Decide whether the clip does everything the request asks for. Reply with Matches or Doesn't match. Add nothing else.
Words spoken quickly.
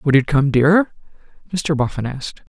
Doesn't match